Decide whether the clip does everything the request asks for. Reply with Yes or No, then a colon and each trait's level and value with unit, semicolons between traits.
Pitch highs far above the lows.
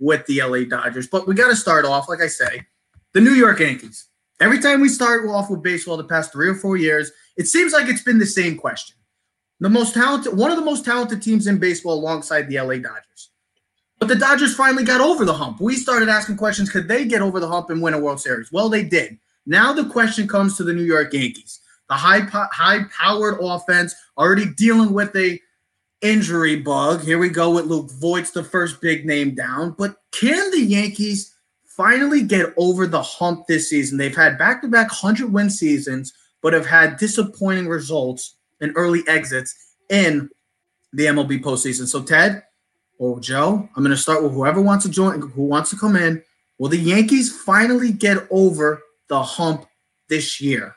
Yes: wide, 5.8 semitones